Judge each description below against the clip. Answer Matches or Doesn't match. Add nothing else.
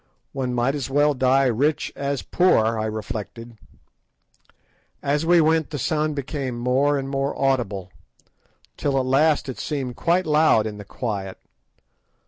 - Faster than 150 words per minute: Doesn't match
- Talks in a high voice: Doesn't match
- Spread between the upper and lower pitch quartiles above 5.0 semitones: Doesn't match